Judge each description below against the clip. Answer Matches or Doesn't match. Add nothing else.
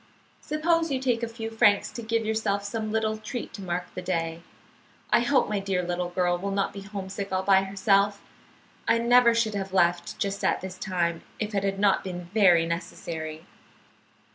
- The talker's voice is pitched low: Doesn't match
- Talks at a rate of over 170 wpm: Matches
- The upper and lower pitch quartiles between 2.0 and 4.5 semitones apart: Matches